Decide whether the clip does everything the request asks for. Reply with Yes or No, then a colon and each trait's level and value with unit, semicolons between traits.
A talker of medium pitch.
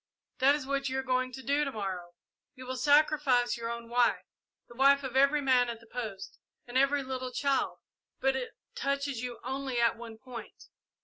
No: very high, 260 Hz